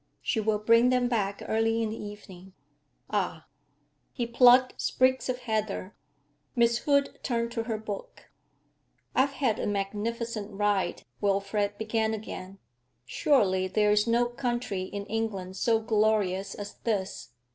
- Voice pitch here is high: Yes, high, 220 Hz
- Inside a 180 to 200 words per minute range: No, slow, 135 wpm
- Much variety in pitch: No, average, 2.7 semitones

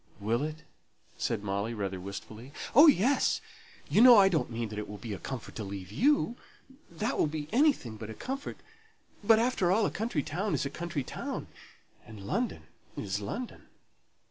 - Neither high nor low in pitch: Yes, medium, 145 Hz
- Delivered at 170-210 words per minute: Yes, average, 180 wpm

